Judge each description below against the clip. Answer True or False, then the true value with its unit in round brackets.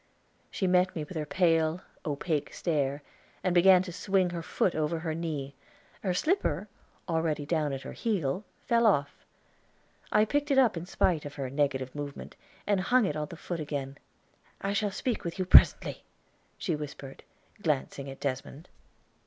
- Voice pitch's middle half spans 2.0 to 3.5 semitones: False (4.4 semitones)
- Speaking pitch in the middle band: True (165 Hz)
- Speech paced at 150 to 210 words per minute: True (170 wpm)